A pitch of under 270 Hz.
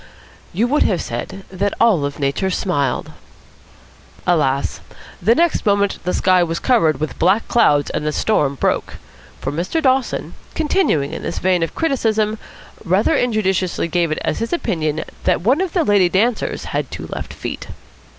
Yes: high, 190 Hz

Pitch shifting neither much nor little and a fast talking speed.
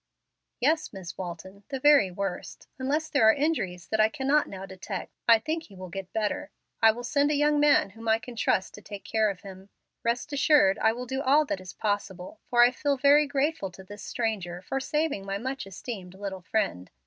No: wide, 6.4 semitones; fast, 210 wpm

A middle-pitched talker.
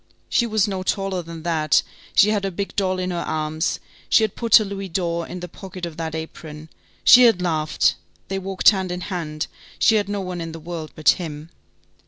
Yes: medium, 180 Hz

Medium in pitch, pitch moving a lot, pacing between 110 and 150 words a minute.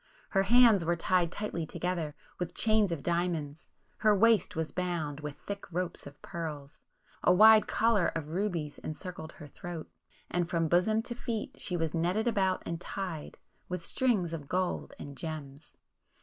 No: medium, 175 Hz; average, 3.9 semitones; average, 145 wpm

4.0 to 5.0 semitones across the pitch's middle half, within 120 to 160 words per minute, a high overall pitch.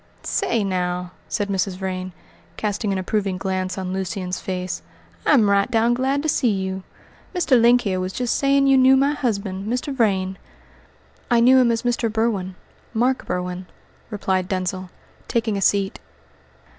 Yes: average, 4.3 semitones; average, 155 wpm; high, 200 Hz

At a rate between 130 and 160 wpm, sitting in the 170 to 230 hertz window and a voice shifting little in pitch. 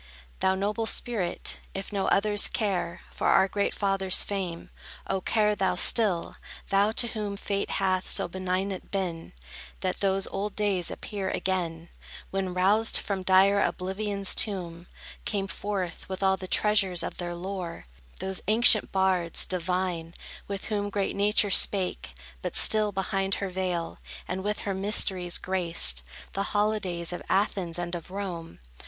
Yes: average, 150 wpm; high, 190 Hz; narrow, 2.0 semitones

